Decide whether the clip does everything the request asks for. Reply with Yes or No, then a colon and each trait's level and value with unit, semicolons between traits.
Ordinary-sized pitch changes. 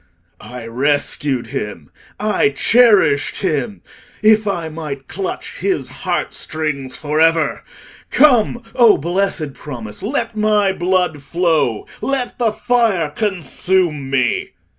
No: wide, 7.0 semitones